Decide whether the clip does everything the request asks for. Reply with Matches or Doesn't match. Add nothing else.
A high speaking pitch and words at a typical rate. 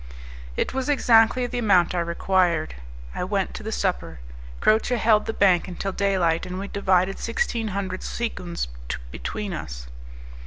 Matches